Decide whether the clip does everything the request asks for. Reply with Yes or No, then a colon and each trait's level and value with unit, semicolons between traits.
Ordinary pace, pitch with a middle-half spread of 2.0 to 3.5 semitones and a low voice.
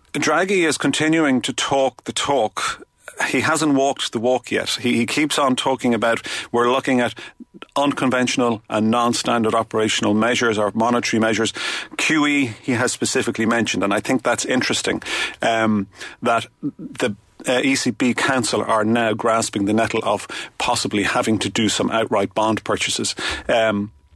Yes: average, 150 wpm; average, 2.8 semitones; low, 120 Hz